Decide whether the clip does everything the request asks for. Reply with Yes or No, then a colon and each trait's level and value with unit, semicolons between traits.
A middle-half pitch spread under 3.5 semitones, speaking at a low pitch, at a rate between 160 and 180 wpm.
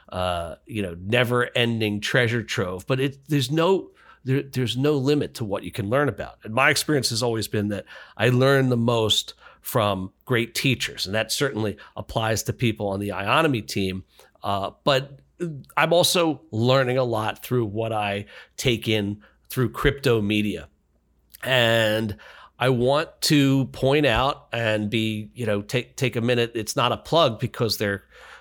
No: average, 4.1 semitones; low, 120 Hz; average, 170 wpm